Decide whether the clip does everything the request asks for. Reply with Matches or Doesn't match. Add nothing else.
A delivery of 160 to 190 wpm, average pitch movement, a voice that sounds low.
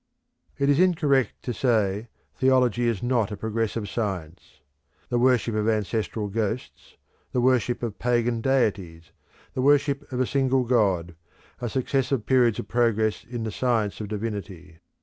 Doesn't match